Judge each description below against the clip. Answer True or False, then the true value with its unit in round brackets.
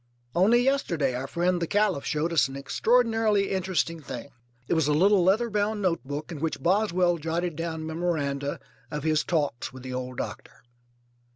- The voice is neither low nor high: True (170 Hz)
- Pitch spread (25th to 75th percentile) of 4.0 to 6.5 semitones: True (4.7 semitones)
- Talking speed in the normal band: True (170 wpm)